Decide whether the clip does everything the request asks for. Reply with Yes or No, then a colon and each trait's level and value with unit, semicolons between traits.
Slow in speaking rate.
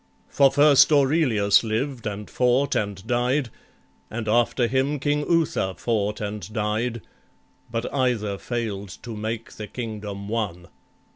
Yes: slow, 130 wpm